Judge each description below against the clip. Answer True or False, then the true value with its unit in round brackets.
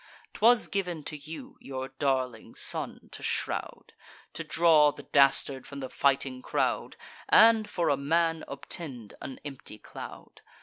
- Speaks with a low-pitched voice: False (145 Hz)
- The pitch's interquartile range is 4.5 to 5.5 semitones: False (3.7 semitones)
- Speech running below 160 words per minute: True (140 wpm)